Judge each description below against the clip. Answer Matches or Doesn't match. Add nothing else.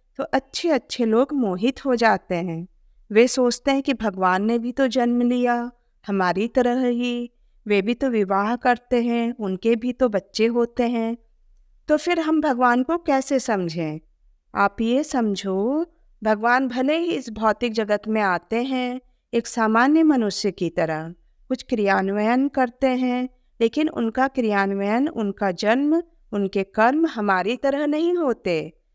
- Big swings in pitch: Doesn't match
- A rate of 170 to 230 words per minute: Doesn't match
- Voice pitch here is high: Matches